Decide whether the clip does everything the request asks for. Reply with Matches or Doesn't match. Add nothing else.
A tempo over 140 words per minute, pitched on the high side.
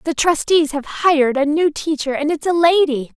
Matches